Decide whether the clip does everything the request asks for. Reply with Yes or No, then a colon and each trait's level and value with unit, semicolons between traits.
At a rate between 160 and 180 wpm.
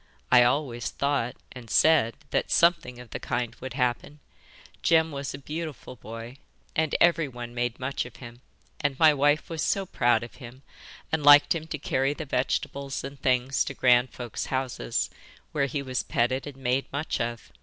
Yes: average, 175 wpm